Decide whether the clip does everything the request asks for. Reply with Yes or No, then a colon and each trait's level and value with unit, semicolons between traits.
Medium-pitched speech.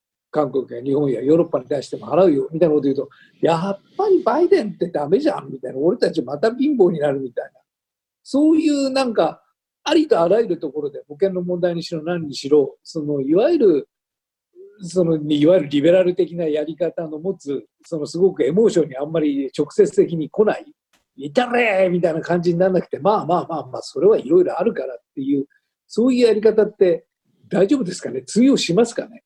Yes: medium, 180 Hz